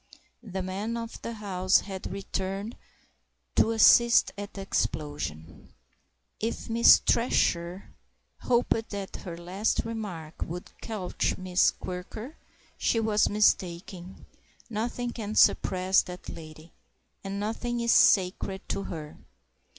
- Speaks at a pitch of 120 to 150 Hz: No, high, 195 Hz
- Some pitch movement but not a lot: Yes, average, 3.7 semitones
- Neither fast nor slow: No, slow, 115 wpm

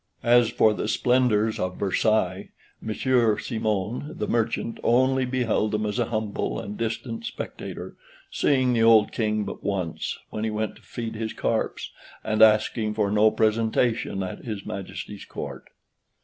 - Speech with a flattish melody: Yes, narrow, 1.8 semitones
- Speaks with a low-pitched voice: Yes, low, 110 Hz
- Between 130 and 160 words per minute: Yes, average, 150 wpm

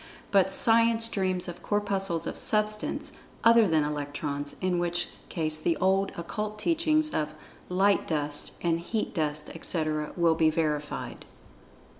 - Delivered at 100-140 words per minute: Yes, slow, 135 wpm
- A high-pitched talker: No, medium, 175 Hz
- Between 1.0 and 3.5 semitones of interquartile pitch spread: No, average, 5.2 semitones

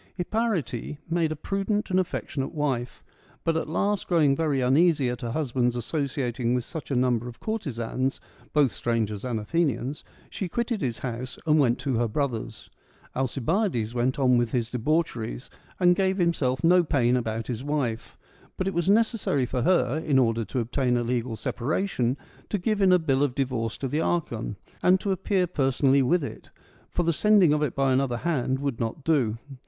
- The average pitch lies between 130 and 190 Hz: Yes, low, 135 Hz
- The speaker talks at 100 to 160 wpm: No, average, 190 wpm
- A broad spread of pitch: Yes, wide, 5.7 semitones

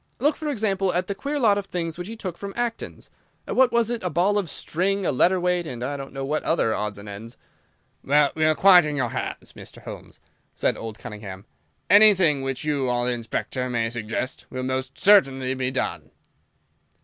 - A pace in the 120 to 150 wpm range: No, average, 195 wpm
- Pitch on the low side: No, medium, 155 Hz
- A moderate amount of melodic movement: No, wide, 7.6 semitones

